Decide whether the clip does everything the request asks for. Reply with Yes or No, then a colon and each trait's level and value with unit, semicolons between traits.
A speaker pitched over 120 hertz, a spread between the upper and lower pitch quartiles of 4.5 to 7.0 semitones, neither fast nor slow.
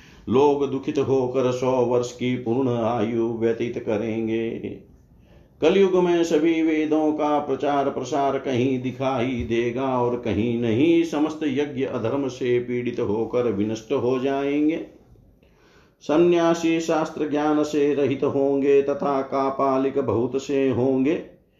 No: low, 135 Hz; average, 3.1 semitones; average, 120 wpm